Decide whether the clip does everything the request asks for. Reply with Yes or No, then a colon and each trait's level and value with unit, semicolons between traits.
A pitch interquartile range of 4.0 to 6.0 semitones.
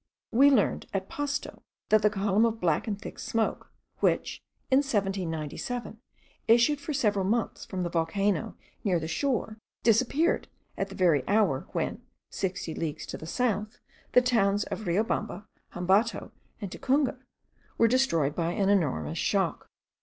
Yes: average, 4.7 semitones